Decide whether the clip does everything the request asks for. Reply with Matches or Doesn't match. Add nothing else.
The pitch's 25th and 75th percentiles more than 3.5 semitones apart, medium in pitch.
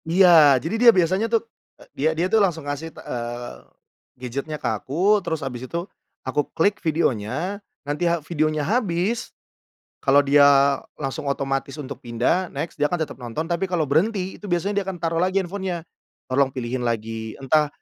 Matches